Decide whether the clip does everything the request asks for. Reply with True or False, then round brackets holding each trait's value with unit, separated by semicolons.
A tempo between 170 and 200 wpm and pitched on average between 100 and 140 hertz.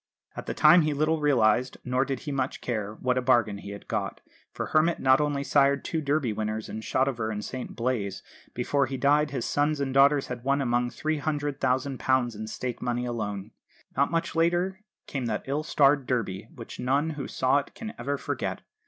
True (195 wpm; 135 Hz)